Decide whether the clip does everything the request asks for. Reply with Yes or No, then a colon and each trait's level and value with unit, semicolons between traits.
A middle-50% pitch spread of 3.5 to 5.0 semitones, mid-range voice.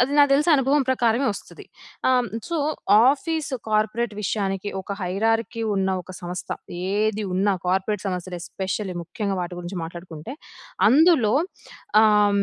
No: average, 4.7 semitones; high, 210 Hz